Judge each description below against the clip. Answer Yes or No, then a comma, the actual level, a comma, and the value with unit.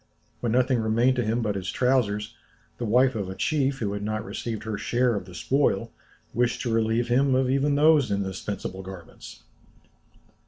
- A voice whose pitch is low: Yes, low, 115 Hz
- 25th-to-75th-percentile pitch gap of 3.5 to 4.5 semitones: Yes, average, 3.8 semitones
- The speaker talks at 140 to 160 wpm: No, average, 175 wpm